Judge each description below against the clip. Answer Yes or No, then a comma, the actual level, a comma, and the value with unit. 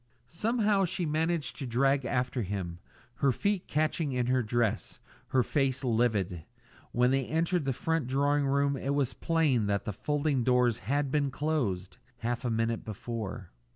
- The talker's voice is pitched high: No, low, 130 Hz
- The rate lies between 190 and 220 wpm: No, average, 160 wpm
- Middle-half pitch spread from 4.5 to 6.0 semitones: No, average, 4.1 semitones